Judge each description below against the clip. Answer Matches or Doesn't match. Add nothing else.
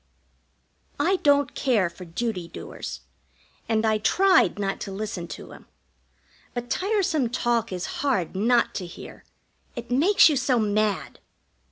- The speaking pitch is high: Matches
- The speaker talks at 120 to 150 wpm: Matches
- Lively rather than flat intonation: Matches